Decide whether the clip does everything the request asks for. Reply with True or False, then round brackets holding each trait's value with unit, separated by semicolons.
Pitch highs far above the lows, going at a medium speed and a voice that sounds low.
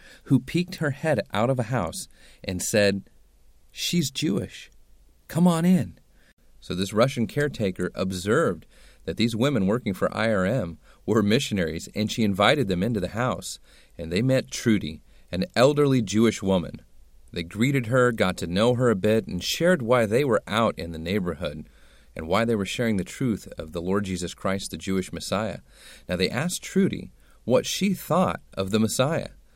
True (6.7 semitones; 175 wpm; 105 Hz)